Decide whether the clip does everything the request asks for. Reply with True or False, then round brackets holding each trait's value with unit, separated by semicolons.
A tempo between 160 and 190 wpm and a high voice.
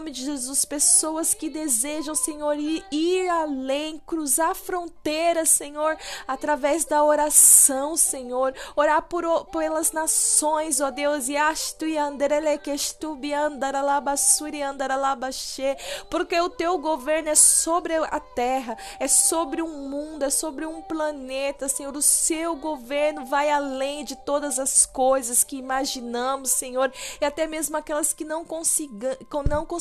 False (135 wpm; 300 Hz)